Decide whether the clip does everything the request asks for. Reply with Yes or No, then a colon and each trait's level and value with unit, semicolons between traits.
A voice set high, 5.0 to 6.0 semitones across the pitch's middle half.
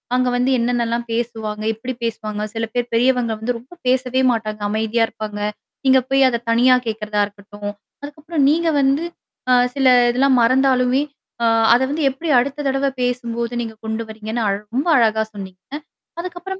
No: high, 240 Hz; average, 3.2 semitones